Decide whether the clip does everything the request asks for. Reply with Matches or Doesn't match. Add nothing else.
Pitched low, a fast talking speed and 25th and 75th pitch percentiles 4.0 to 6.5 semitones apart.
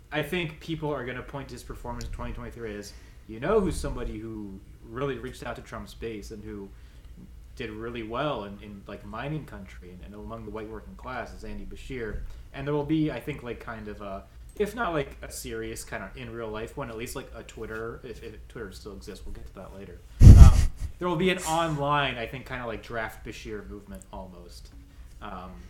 Matches